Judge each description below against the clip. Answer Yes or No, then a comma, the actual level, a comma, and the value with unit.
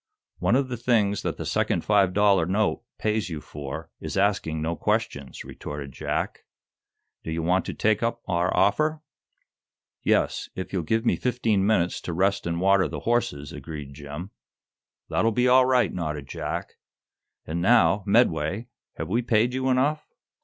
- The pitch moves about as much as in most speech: No, wide, 6.1 semitones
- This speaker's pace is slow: No, average, 165 wpm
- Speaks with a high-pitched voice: No, low, 100 Hz